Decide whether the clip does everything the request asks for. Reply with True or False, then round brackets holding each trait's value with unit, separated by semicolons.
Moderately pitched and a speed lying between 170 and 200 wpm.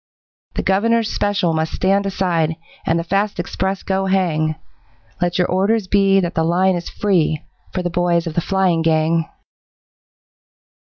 False (180 Hz; 155 wpm)